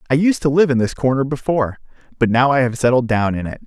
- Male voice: Yes, male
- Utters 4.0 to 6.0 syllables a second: No, 6.5 syllables/s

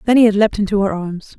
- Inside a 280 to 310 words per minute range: Yes, fast, 305 wpm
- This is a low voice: No, high, 205 Hz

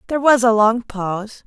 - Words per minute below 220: Yes, fast, 205 wpm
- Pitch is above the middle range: Yes, high, 230 Hz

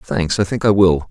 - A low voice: Yes, very low, 95 Hz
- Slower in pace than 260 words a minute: No, fast, 270 wpm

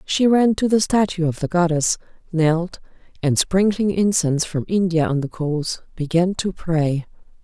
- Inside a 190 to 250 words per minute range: No, average, 160 wpm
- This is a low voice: No, medium, 175 Hz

